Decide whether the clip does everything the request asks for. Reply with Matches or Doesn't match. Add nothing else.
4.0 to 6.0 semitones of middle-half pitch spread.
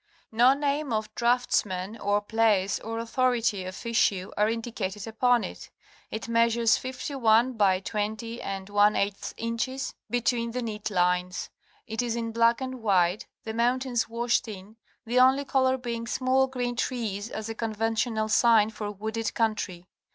Doesn't match